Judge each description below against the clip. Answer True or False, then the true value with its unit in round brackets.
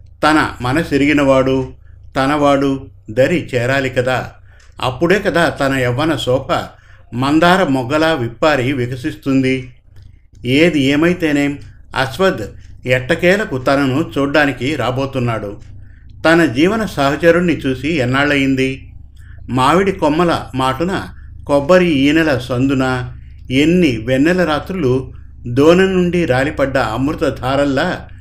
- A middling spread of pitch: True (4.0 semitones)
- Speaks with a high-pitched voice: False (135 Hz)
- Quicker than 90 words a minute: False (85 wpm)